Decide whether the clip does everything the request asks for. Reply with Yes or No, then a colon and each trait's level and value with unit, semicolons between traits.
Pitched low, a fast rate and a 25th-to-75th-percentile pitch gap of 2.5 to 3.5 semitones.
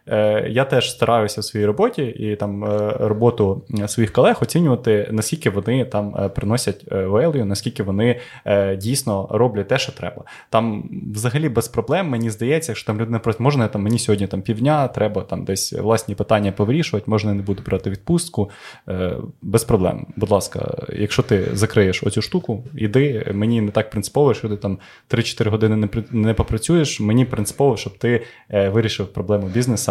Yes: low, 110 Hz; fast, 160 wpm; average, 2.9 semitones